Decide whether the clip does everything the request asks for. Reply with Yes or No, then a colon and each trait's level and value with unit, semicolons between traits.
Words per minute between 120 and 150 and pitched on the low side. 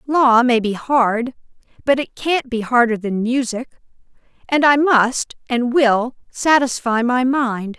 No: average, 145 wpm; very high, 250 Hz